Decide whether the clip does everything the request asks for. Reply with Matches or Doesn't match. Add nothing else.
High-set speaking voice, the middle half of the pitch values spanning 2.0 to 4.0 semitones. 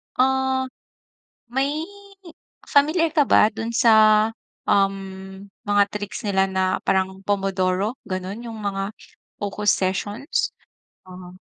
Matches